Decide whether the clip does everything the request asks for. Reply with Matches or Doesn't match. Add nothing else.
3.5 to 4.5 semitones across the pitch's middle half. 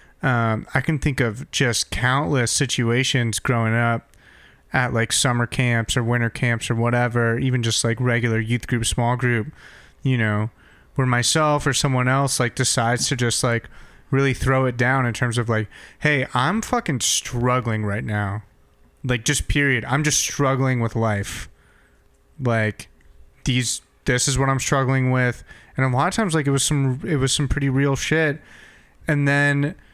Doesn't match